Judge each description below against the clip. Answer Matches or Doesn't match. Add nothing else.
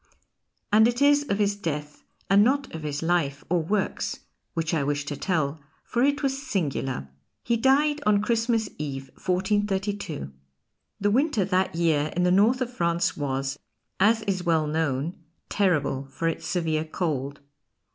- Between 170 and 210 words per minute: Doesn't match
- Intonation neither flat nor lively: Doesn't match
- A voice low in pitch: Doesn't match